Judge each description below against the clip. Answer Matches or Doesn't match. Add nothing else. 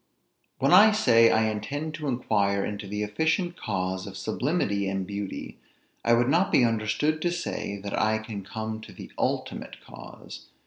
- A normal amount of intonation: Doesn't match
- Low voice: Matches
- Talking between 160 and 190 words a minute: Matches